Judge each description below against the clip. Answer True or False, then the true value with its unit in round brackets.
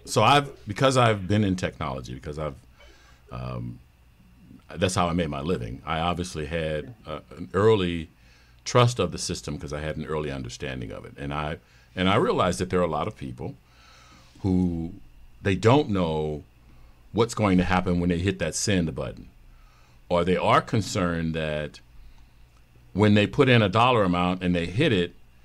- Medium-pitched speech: False (85 Hz)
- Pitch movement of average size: False (7.1 semitones)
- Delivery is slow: False (180 wpm)